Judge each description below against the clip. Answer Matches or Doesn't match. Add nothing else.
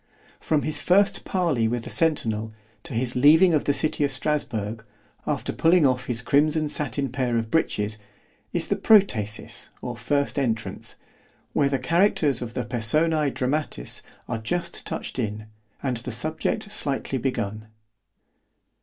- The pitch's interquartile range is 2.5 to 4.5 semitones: Doesn't match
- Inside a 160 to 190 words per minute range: Doesn't match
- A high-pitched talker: Doesn't match